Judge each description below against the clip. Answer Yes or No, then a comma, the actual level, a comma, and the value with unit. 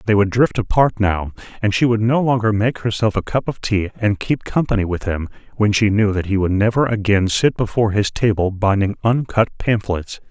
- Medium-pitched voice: No, low, 105 Hz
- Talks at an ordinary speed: No, fast, 210 wpm